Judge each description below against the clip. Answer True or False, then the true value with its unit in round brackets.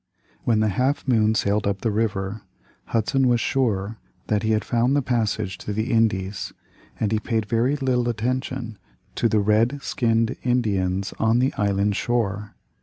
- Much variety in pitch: False (2.8 semitones)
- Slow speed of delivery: False (165 wpm)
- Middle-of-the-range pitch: False (110 Hz)